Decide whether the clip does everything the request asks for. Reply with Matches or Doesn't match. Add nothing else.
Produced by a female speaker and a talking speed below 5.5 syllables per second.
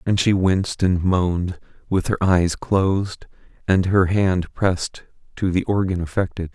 Doesn't match